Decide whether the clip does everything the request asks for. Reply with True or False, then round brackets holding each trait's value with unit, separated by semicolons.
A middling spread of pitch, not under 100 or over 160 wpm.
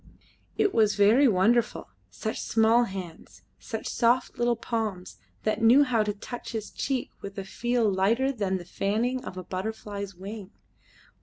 True (3.4 semitones; 155 wpm)